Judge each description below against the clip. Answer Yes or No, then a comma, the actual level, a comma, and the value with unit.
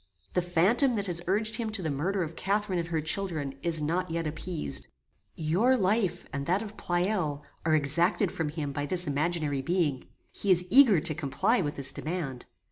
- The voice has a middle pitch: Yes, medium, 170 Hz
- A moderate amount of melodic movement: Yes, average, 4.4 semitones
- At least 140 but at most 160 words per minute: No, average, 190 wpm